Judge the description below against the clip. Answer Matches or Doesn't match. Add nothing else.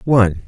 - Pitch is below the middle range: Matches